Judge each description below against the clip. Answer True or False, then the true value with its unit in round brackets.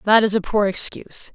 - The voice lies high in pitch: True (205 Hz)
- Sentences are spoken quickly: True (225 wpm)